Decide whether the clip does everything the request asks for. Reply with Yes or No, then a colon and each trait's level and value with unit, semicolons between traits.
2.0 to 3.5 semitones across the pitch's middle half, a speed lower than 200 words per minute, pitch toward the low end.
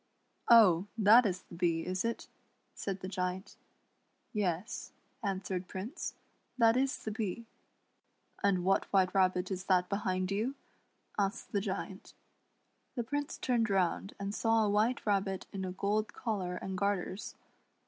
No: average, 2.8 semitones; average, 165 wpm; high, 195 Hz